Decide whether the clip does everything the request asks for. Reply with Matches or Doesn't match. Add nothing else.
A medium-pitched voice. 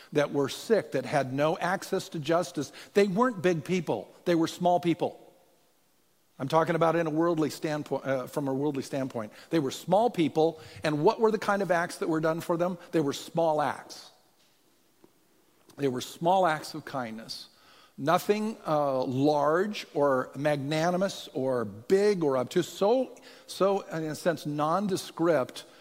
Matches